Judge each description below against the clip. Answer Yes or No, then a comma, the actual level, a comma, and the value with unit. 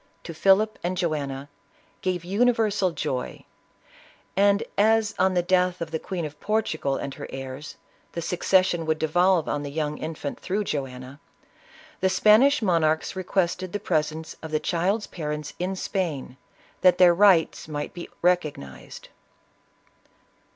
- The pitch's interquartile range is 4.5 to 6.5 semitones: No, average, 3.9 semitones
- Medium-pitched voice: Yes, medium, 175 Hz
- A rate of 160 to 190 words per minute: No, average, 140 wpm